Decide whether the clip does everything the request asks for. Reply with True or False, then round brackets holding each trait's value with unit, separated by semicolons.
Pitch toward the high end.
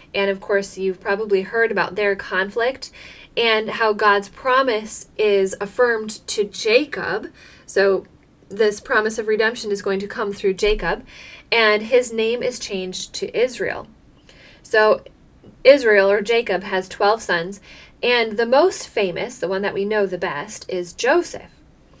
True (210 Hz)